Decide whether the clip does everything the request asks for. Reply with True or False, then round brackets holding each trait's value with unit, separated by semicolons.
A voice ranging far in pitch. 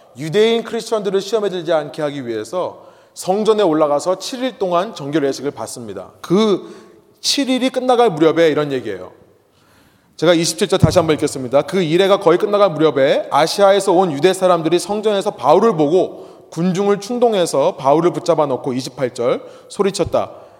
False (5.0 semitones)